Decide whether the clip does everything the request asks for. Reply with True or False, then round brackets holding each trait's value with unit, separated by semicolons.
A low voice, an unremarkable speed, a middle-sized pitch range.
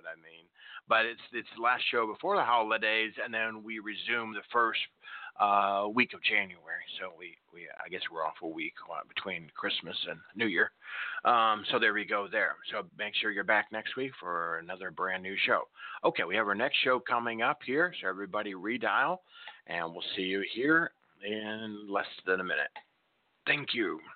False (105 Hz; 190 wpm; 1.8 semitones)